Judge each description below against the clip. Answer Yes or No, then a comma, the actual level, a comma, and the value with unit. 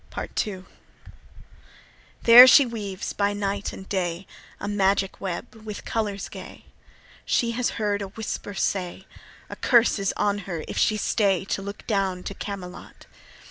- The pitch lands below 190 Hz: No, high, 200 Hz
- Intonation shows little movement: Yes, narrow, 1.9 semitones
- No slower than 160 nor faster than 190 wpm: No, average, 150 wpm